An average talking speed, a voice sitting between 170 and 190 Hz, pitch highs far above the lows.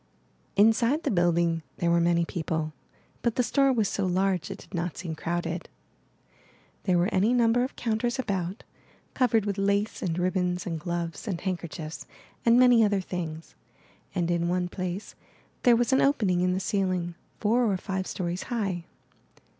No: average, 165 wpm; medium, 185 Hz; average, 4.2 semitones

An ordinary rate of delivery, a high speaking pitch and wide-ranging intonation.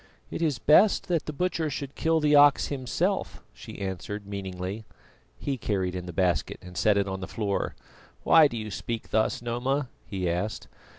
No: average, 180 wpm; low, 110 Hz; wide, 7.0 semitones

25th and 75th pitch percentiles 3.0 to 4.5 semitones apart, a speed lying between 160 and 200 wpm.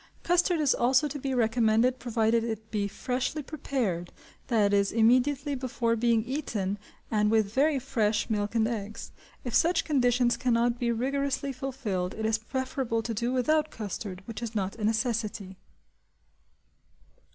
No: average, 3.3 semitones; average, 150 wpm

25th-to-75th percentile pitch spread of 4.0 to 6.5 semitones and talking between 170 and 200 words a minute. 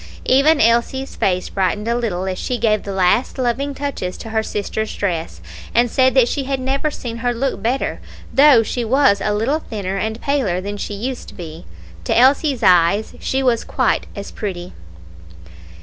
Yes: average, 4.9 semitones; average, 180 wpm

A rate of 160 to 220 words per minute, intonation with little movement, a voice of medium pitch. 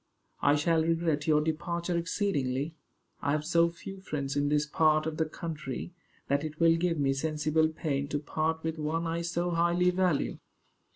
Yes: average, 175 wpm; narrow, 2.2 semitones; medium, 160 Hz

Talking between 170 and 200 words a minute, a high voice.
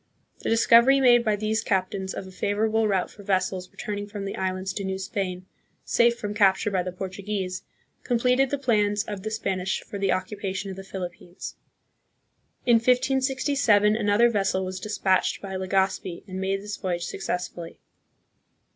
No: average, 160 wpm; high, 200 Hz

